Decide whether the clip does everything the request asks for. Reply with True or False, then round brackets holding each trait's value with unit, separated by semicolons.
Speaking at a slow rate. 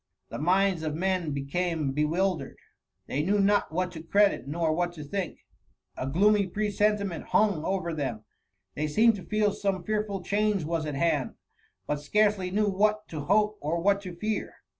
False (180 wpm)